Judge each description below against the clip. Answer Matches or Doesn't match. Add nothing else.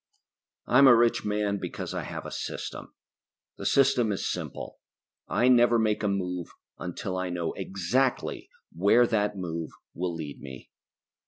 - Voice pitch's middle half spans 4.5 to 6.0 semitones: Matches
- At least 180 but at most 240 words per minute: Doesn't match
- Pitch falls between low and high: Doesn't match